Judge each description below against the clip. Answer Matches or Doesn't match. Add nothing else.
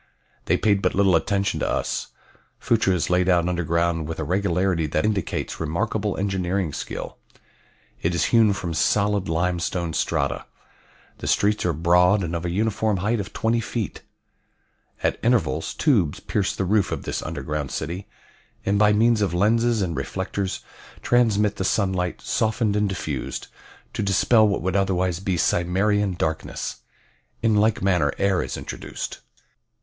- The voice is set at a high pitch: Doesn't match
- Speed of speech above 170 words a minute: Doesn't match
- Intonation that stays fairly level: Doesn't match